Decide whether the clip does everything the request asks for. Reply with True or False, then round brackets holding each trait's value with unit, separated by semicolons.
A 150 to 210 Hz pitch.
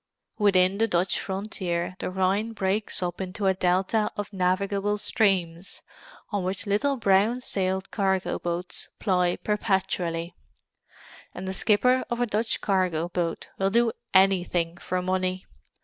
True (190 Hz)